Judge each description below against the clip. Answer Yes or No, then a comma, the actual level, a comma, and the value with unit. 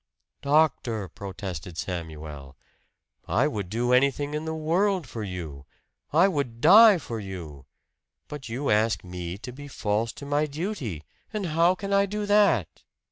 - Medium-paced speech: Yes, average, 150 wpm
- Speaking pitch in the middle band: No, low, 125 Hz